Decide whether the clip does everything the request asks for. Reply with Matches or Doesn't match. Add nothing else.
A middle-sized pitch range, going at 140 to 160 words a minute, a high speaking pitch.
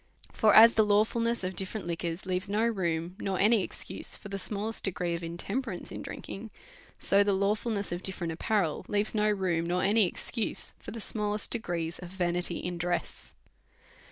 Doesn't match